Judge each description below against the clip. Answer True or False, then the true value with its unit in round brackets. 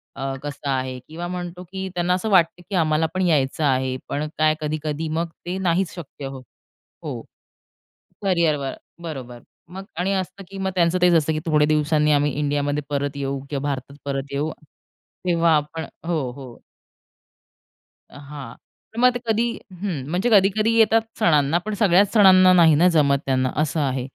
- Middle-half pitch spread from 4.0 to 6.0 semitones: True (4.3 semitones)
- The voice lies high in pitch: False (155 Hz)